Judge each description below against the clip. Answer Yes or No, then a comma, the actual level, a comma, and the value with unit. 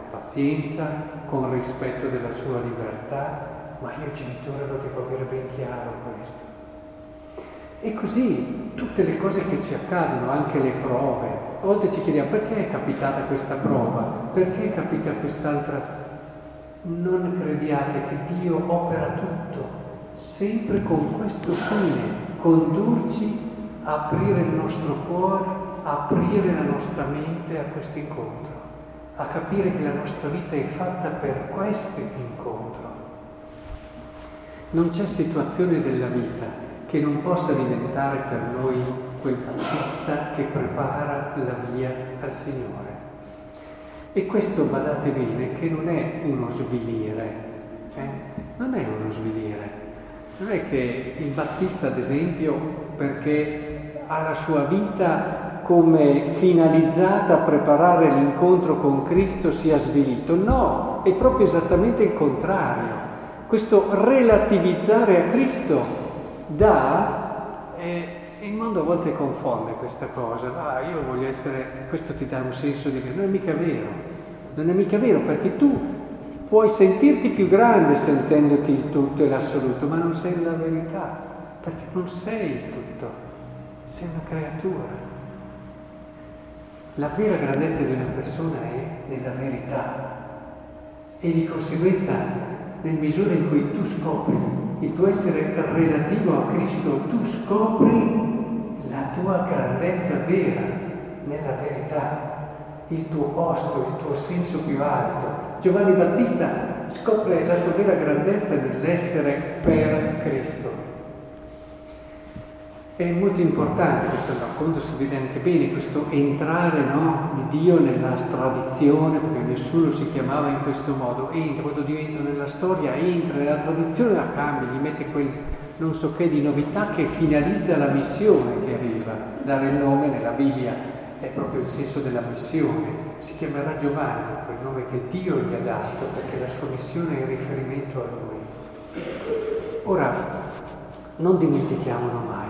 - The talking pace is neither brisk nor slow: Yes, average, 135 wpm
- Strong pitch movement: No, average, 4.4 semitones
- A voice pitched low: No, medium, 155 Hz